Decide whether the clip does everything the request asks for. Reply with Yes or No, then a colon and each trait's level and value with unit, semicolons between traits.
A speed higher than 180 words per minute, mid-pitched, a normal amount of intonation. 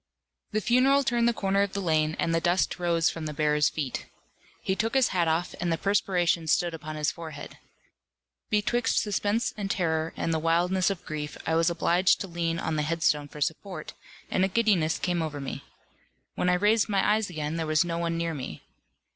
Yes: fast, 205 wpm; medium, 170 Hz; average, 3.8 semitones